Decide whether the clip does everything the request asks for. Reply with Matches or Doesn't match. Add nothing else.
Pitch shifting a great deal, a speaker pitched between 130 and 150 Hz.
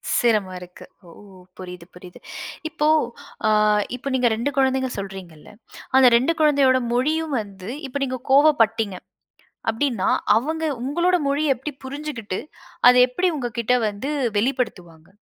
Doesn't match